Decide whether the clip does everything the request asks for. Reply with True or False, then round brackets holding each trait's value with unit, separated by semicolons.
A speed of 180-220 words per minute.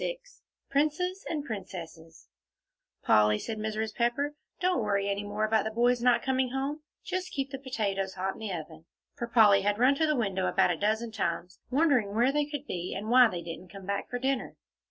True (200 wpm)